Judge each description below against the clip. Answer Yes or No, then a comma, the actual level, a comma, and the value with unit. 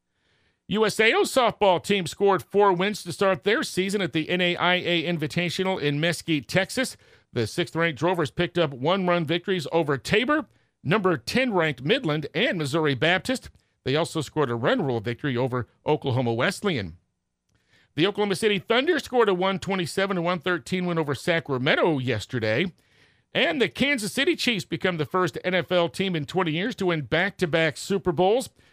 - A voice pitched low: No, medium, 175 Hz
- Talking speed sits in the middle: Yes, average, 165 wpm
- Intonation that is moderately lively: Yes, average, 3.9 semitones